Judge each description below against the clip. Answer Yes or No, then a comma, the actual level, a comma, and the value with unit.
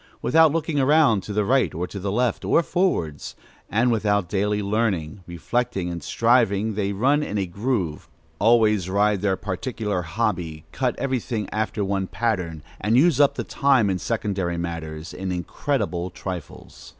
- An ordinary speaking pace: Yes, average, 160 wpm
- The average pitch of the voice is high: No, low, 105 Hz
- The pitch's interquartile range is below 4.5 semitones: No, average, 4.8 semitones